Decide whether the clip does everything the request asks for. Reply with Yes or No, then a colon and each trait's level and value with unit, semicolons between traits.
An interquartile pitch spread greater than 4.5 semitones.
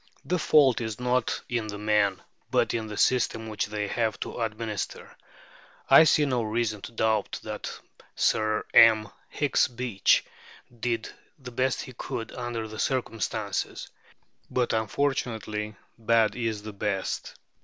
No: narrow, 2.4 semitones